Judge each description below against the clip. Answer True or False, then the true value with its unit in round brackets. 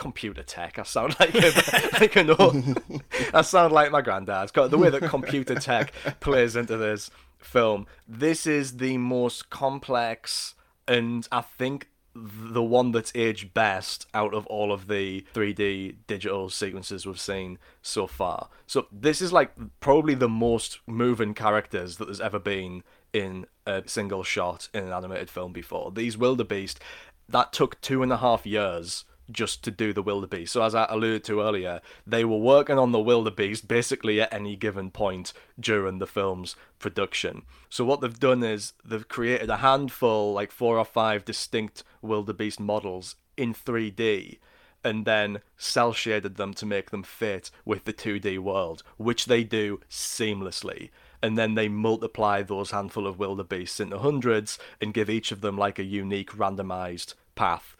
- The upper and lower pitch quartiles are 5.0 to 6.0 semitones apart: False (3.0 semitones)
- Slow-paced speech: False (165 wpm)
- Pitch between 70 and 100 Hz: False (110 Hz)